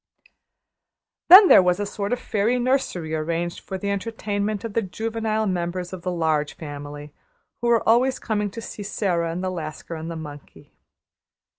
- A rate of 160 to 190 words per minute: Yes, average, 170 wpm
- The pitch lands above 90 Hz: Yes, high, 190 Hz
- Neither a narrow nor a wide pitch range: Yes, average, 4.8 semitones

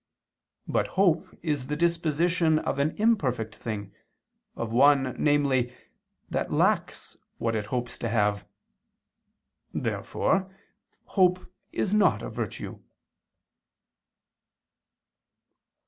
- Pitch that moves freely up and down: Yes, wide, 6.4 semitones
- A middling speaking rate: No, slow, 95 wpm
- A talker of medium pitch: Yes, medium, 145 Hz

